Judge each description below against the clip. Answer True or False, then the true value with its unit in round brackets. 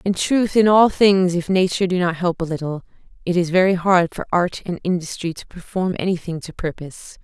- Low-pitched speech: False (180 Hz)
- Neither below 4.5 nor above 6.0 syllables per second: True (5.5 syllables/s)